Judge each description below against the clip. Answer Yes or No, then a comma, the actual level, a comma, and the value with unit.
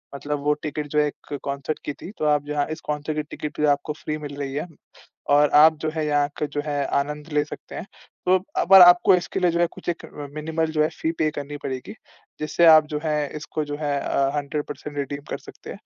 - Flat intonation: Yes, narrow, 1.4 semitones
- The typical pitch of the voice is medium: Yes, medium, 150 Hz